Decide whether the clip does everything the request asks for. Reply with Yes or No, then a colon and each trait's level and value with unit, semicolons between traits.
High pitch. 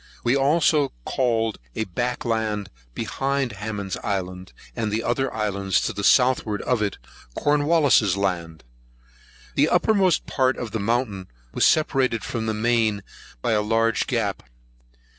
No: low, 115 Hz